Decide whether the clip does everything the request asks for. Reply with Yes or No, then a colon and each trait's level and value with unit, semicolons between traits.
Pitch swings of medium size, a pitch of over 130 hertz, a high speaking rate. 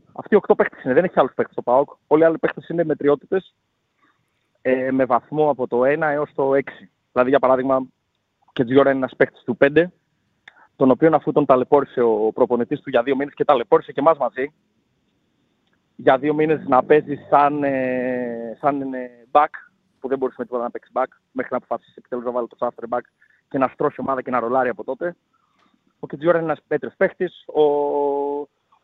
Yes: average, 3.0 semitones; medium, 140 Hz; fast, 195 wpm